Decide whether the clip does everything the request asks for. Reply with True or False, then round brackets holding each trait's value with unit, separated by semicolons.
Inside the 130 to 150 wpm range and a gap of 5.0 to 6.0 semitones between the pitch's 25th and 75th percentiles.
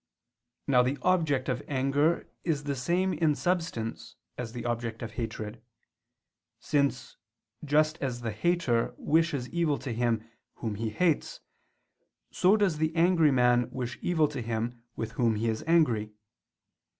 True (145 wpm; 5.4 semitones)